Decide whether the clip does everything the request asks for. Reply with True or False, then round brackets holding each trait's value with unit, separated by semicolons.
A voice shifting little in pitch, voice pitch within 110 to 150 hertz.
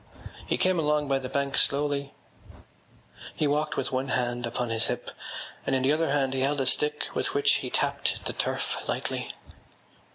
True (2.1 semitones; 140 Hz)